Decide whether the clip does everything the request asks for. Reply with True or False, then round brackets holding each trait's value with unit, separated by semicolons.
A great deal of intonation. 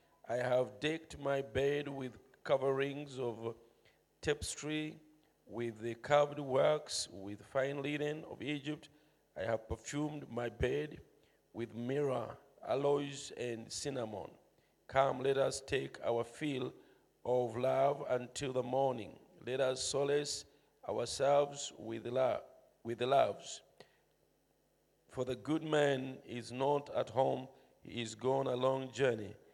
False (3.1 semitones)